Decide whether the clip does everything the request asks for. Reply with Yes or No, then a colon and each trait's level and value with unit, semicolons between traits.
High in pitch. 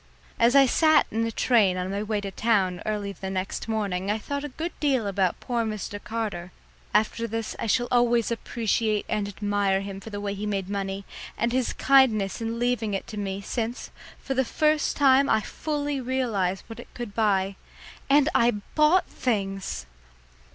Yes: high, 220 Hz